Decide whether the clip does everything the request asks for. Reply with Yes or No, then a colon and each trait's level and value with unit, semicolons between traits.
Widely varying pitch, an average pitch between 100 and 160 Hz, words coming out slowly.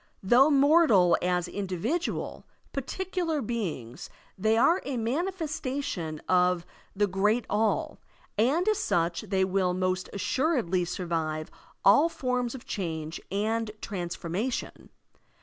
No: wide, 7.2 semitones; high, 210 Hz; slow, 110 wpm